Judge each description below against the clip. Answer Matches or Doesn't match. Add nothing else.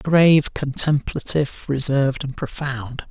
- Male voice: Matches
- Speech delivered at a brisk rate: Doesn't match